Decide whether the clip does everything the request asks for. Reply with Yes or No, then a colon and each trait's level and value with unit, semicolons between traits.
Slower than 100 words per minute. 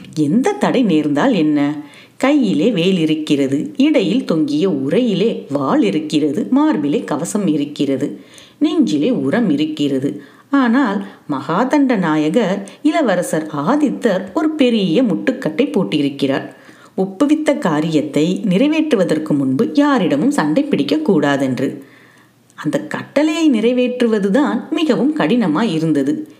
Yes: average, 90 wpm